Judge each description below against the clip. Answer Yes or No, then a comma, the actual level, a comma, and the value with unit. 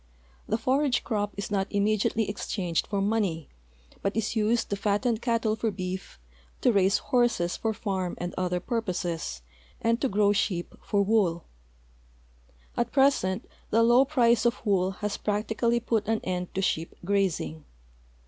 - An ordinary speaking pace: Yes, average, 150 wpm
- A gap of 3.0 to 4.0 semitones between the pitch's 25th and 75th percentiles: Yes, average, 3.5 semitones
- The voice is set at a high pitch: Yes, high, 205 Hz